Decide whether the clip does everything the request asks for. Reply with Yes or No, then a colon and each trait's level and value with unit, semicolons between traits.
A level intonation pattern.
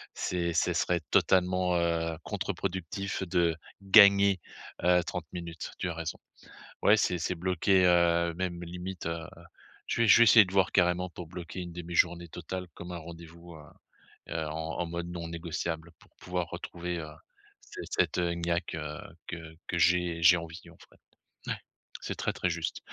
Yes: narrow, 1.4 semitones